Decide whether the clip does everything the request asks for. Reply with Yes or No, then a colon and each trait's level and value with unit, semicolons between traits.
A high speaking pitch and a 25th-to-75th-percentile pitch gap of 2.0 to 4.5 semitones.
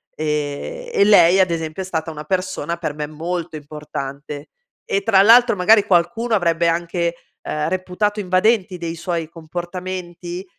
No: medium, 175 Hz; average, 2.9 semitones